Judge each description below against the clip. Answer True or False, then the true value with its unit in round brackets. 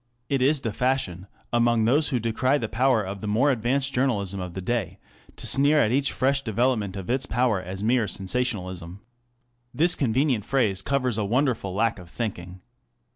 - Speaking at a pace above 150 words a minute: True (180 wpm)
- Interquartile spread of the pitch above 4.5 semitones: True (5.0 semitones)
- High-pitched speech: False (115 Hz)